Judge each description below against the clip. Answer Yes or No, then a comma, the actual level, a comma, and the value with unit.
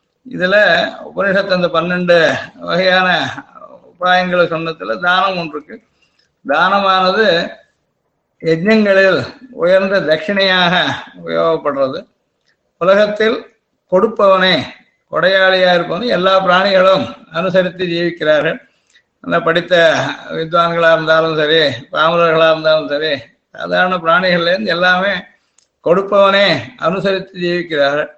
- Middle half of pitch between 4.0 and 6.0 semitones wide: No, average, 2.9 semitones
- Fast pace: No, average, 80 wpm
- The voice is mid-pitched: Yes, medium, 180 Hz